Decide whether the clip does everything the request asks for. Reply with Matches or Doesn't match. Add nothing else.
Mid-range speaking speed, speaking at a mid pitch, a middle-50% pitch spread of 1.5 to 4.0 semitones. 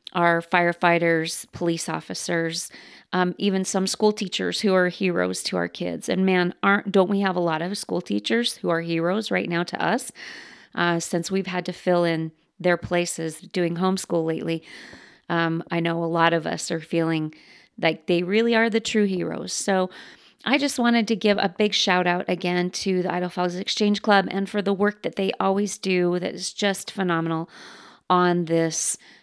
Matches